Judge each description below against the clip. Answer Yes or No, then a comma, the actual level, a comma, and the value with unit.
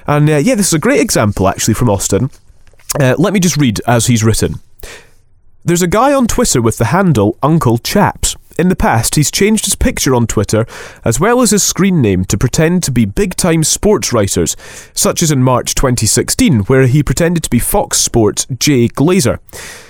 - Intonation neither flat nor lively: No, wide, 6.8 semitones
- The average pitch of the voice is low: Yes, low, 130 Hz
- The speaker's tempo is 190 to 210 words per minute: Yes, average, 200 wpm